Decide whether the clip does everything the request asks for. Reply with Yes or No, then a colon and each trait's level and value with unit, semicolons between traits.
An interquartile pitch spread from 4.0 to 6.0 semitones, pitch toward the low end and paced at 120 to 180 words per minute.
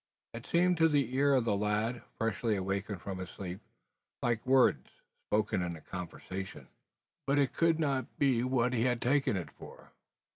Yes: wide, 5.6 semitones; low, 115 Hz; average, 170 wpm